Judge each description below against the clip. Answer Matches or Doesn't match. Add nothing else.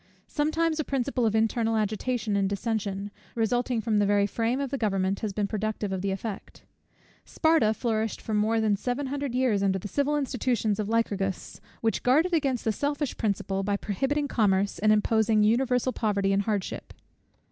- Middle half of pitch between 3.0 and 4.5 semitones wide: Matches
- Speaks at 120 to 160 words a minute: Doesn't match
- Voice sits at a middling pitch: Doesn't match